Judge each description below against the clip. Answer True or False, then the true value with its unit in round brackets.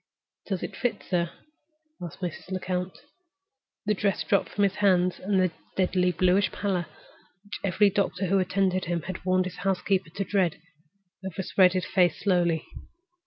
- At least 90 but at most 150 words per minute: True (145 wpm)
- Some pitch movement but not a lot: False (1.6 semitones)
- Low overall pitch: False (185 Hz)